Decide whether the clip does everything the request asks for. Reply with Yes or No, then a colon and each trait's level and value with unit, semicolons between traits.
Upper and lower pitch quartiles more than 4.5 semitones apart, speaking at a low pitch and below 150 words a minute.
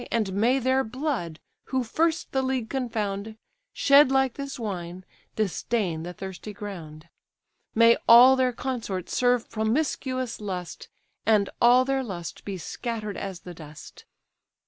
No: average, 5.2 semitones; high, 225 Hz; slow, 135 wpm